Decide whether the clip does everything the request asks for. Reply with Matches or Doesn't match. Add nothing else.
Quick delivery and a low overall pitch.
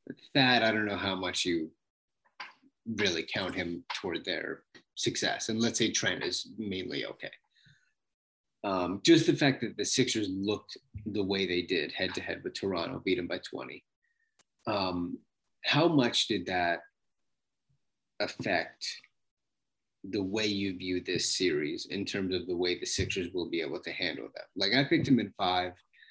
Doesn't match